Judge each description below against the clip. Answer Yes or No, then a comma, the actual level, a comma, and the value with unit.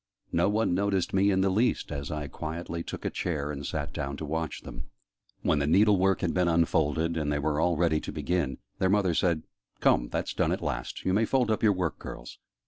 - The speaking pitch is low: Yes, very low, 85 Hz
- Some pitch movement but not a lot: Yes, average, 3.8 semitones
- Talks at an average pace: No, fast, 225 wpm